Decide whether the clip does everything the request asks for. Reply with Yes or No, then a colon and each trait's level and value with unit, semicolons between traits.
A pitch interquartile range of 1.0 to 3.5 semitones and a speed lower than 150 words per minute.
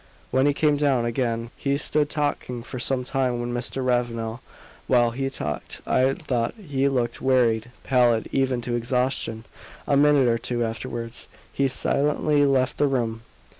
No: narrow, 2.5 semitones; average, 160 wpm